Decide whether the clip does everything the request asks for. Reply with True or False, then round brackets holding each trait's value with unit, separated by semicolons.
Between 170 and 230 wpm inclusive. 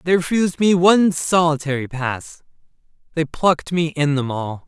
False (155 wpm)